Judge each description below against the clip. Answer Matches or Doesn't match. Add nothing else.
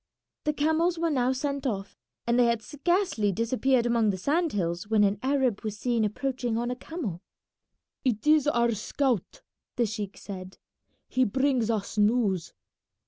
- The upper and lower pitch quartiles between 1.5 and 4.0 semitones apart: Doesn't match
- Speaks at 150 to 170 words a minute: Matches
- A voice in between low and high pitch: Doesn't match